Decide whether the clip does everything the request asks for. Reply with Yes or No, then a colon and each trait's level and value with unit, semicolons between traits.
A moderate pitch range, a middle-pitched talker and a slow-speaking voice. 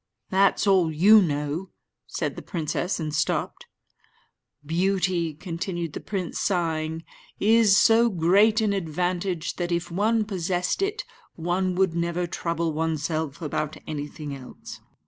Yes: average, 3.2 semitones; medium, 175 Hz; slow, 125 wpm